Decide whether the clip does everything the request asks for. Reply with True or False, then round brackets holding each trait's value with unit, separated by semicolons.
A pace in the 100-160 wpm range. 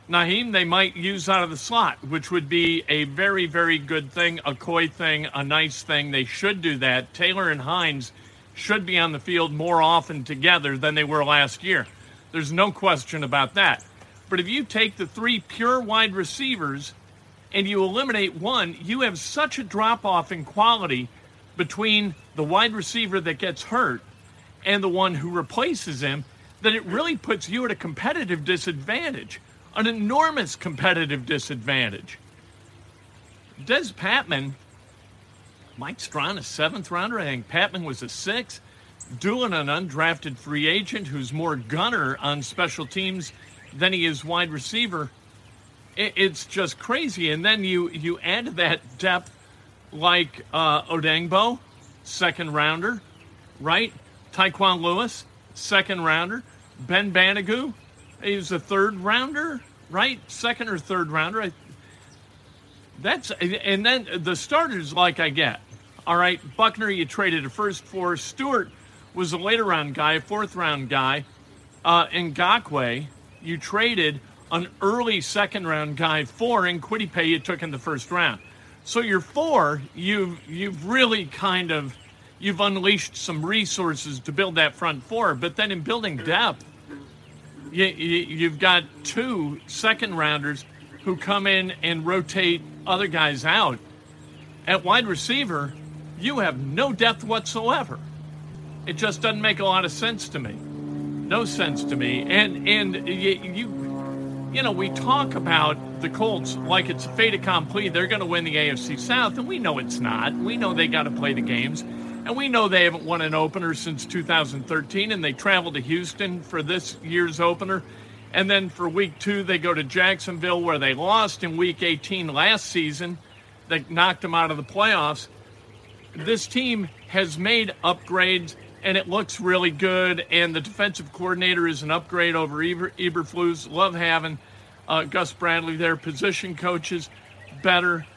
True (155 wpm)